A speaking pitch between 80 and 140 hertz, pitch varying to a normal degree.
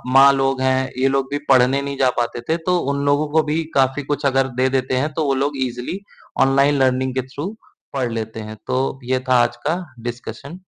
No: low, 135 Hz; narrow, 1.8 semitones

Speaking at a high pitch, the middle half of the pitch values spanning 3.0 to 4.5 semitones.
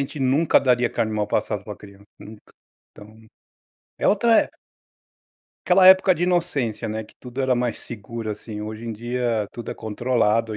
No: low, 115 Hz; average, 3.7 semitones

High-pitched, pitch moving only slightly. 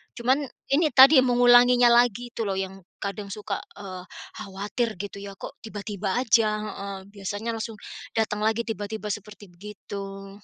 No: high, 210 Hz; average, 3.1 semitones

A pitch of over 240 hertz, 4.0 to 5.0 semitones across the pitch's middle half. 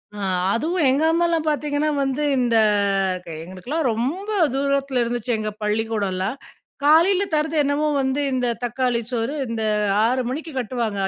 Yes: very high, 260 Hz; average, 4.6 semitones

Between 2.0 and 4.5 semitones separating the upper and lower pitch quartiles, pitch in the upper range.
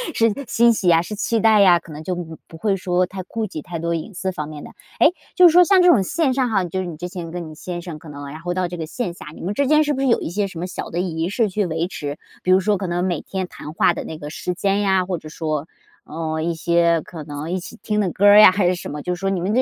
No: average, 3.8 semitones; medium, 180 Hz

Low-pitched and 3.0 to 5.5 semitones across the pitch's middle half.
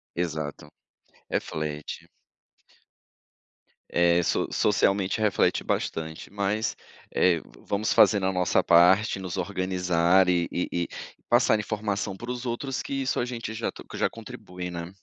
Yes: very low, 95 Hz; average, 3.7 semitones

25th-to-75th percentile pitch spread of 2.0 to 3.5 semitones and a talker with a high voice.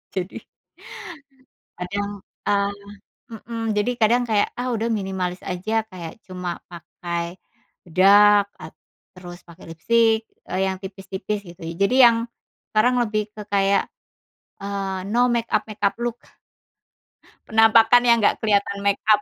Yes: average, 2.9 semitones; high, 205 Hz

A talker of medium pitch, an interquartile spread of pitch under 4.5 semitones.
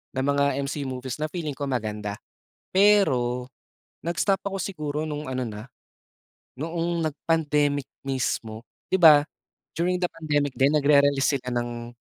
Yes: medium, 145 Hz; average, 4.1 semitones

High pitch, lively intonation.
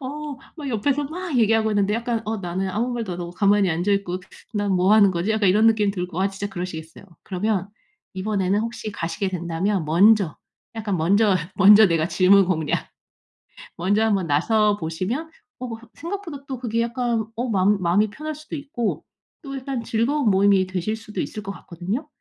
No: high, 205 Hz; average, 3.9 semitones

